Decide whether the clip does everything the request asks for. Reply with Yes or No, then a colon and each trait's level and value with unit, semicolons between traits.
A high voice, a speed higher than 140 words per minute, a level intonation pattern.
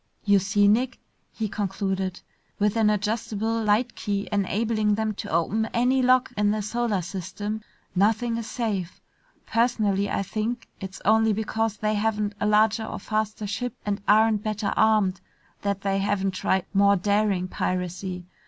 Yes: high, 210 Hz; average, 155 wpm; narrow, 1.9 semitones